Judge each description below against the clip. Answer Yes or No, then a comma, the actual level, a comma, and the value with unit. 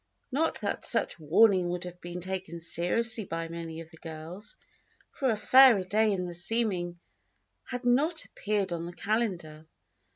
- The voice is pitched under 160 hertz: No, medium, 185 Hz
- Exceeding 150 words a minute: Yes, average, 160 wpm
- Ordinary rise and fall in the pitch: Yes, average, 4.7 semitones